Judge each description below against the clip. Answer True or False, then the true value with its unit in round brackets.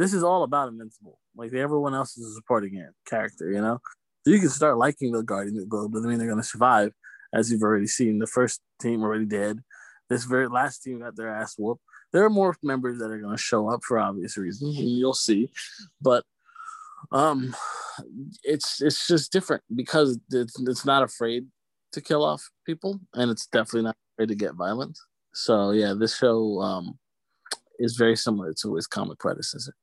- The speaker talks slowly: False (195 wpm)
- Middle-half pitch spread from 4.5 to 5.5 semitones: False (4.1 semitones)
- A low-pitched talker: True (120 Hz)